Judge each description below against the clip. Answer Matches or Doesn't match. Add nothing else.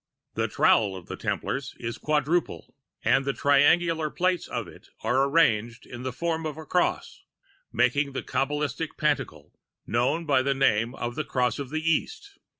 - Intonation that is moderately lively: Matches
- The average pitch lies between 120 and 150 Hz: Matches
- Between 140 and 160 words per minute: Doesn't match